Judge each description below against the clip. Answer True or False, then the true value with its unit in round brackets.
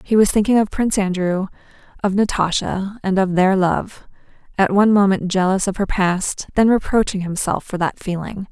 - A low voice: False (195 Hz)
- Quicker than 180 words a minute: False (175 wpm)